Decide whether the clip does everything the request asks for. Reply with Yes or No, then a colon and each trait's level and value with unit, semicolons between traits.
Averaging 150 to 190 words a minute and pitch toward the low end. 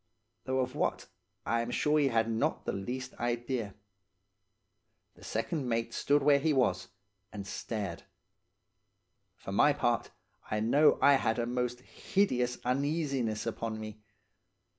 No: average, 140 wpm; low, 125 Hz